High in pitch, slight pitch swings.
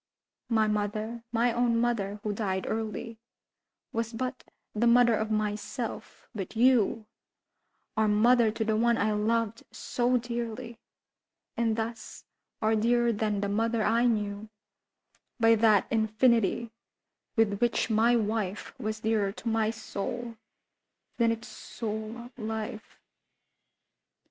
Yes: high, 225 Hz; narrow, 1.6 semitones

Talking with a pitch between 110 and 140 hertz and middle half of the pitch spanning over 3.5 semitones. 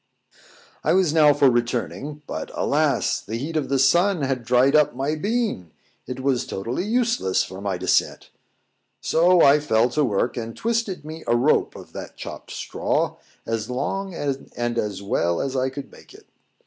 Yes: low, 135 Hz; average, 4.9 semitones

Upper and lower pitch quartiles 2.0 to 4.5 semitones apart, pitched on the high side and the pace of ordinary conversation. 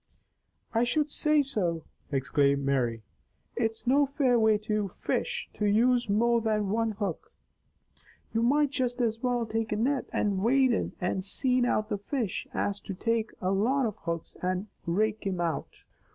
Yes: average, 4.0 semitones; high, 220 Hz; average, 165 wpm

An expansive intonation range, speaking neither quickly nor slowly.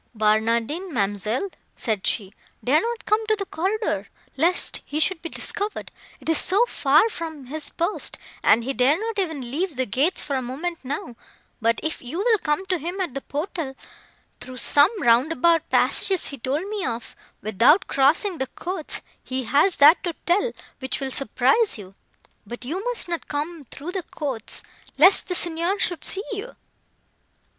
Yes: wide, 6.3 semitones; average, 170 wpm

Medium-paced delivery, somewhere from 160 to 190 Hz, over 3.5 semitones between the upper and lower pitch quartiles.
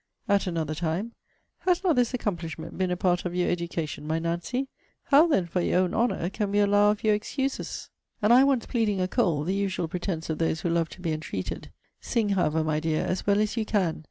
No: fast, 220 wpm; medium, 185 Hz; average, 4.2 semitones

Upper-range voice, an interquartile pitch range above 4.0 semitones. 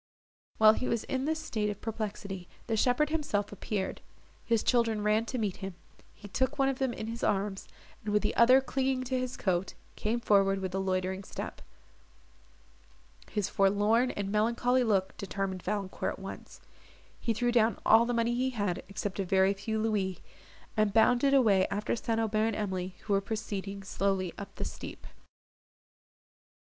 No: high, 215 Hz; average, 3.3 semitones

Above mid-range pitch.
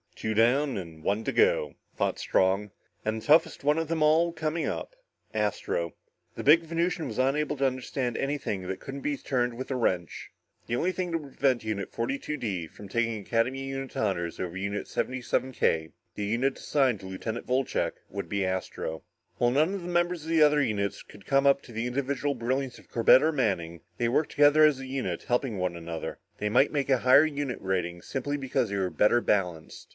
No: low, 125 Hz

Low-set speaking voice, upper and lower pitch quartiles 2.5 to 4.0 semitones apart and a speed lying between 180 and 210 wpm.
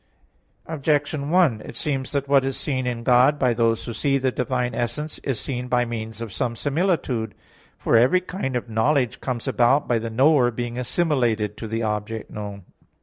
Yes: low, 125 Hz; average, 3.5 semitones; average, 185 wpm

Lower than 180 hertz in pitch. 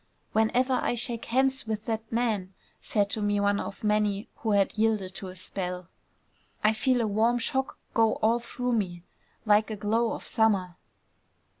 No: high, 220 Hz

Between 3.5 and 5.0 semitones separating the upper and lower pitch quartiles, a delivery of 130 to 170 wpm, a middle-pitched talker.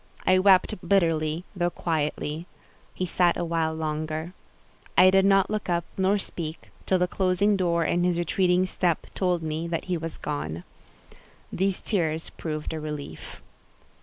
No: average, 2.8 semitones; average, 155 wpm; medium, 170 Hz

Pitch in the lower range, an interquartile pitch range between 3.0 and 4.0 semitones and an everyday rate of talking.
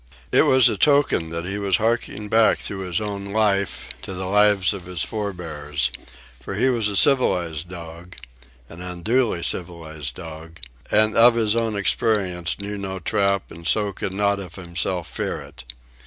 Yes: very low, 95 Hz; average, 3.6 semitones; average, 170 wpm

